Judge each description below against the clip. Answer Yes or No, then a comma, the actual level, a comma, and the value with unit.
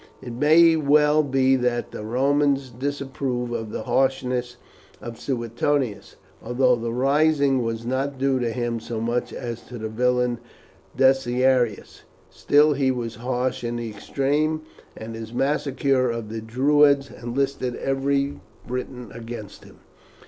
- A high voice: No, low, 125 Hz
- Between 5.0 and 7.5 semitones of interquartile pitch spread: No, average, 2.8 semitones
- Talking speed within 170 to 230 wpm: No, slow, 135 wpm